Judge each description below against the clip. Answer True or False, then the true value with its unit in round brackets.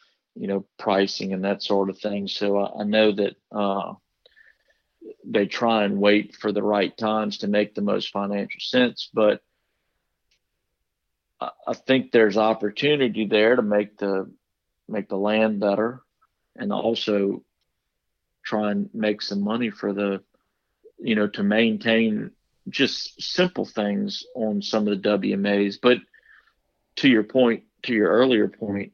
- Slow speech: False (145 wpm)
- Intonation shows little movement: True (1.7 semitones)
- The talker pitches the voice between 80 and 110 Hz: True (105 Hz)